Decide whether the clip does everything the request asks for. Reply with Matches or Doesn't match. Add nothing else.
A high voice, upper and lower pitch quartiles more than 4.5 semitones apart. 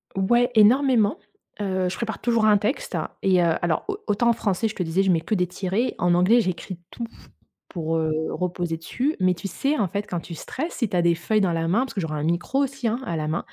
Matches